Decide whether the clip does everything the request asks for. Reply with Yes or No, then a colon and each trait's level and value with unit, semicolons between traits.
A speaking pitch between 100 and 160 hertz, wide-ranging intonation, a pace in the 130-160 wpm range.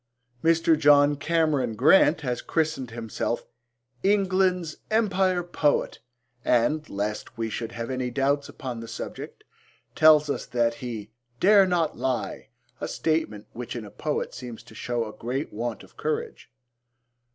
Yes: medium, 140 Hz; wide, 5.8 semitones; average, 140 wpm